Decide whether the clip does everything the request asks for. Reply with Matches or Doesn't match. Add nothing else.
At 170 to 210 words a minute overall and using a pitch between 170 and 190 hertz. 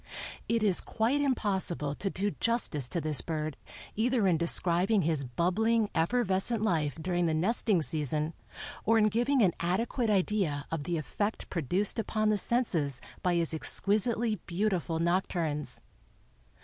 Doesn't match